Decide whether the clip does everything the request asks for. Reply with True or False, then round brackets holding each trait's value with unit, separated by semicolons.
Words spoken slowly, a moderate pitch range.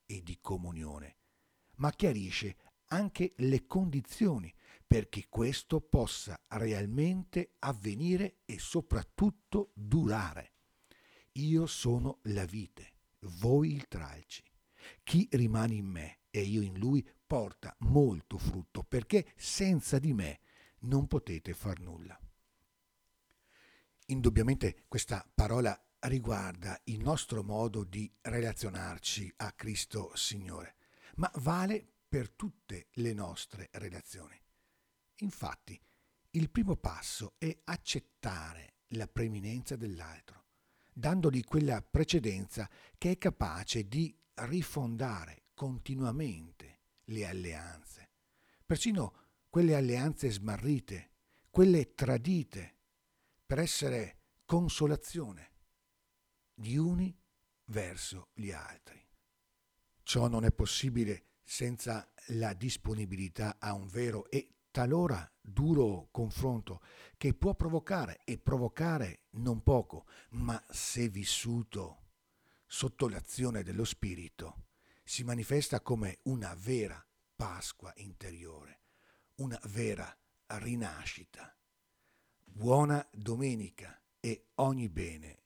False (95 wpm; 6.4 semitones)